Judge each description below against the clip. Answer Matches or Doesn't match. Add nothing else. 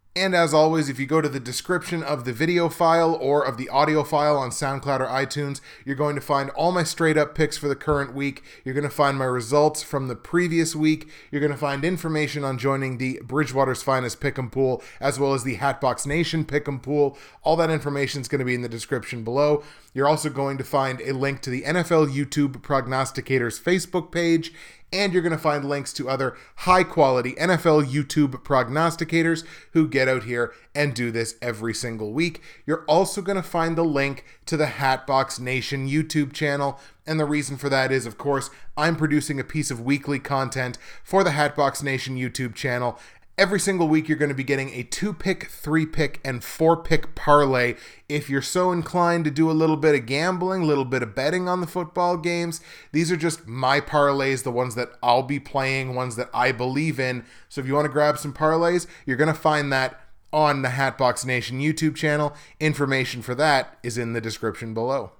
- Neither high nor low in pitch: Matches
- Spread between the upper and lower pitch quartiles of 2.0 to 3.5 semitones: Matches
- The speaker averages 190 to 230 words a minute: Matches